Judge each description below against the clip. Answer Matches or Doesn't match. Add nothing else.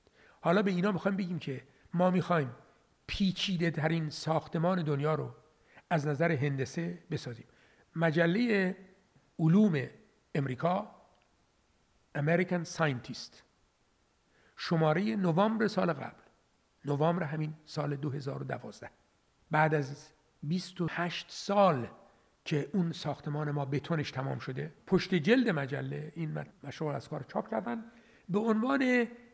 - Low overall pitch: Doesn't match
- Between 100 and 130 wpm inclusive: Matches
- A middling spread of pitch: Matches